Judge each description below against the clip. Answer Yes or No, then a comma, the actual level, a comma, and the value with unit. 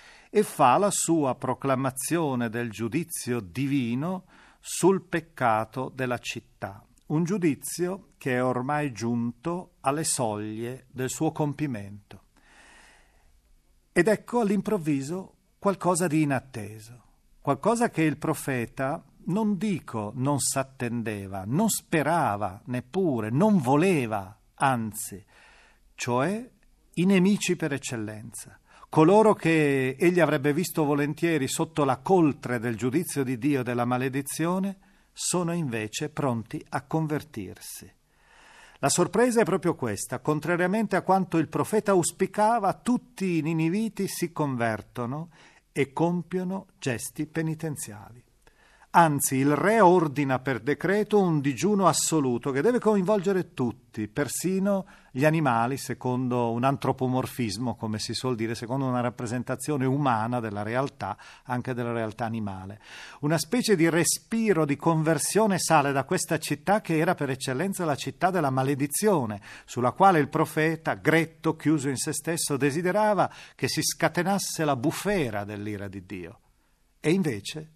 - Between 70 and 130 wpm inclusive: Yes, average, 125 wpm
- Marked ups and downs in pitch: Yes, wide, 5.9 semitones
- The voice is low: No, medium, 145 Hz